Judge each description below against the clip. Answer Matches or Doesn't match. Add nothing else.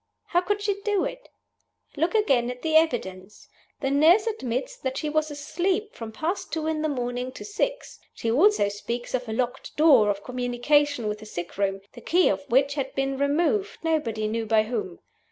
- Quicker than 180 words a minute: Matches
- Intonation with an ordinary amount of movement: Doesn't match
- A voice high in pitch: Matches